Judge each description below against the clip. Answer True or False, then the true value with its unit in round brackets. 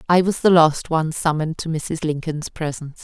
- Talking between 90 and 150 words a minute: False (200 wpm)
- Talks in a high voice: False (160 Hz)